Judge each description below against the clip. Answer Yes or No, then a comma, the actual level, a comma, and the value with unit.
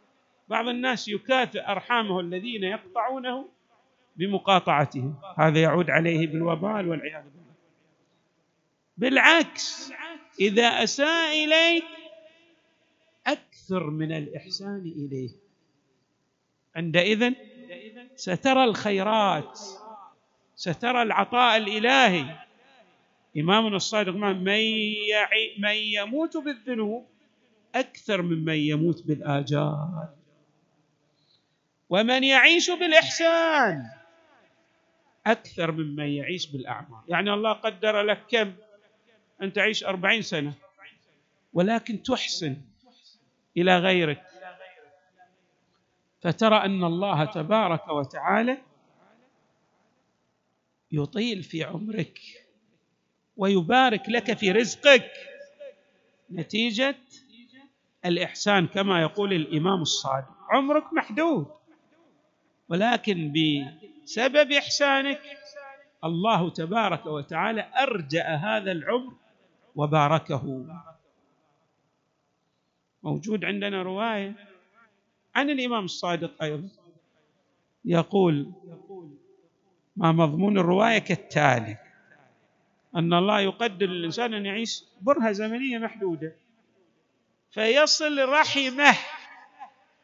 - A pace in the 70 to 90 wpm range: Yes, average, 75 wpm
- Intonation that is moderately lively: No, wide, 6.9 semitones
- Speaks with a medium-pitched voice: No, high, 200 Hz